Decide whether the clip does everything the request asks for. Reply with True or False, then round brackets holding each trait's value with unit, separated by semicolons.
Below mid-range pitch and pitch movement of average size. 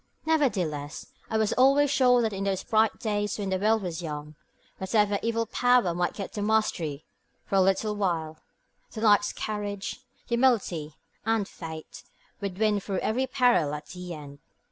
False (205 Hz; 4.2 semitones)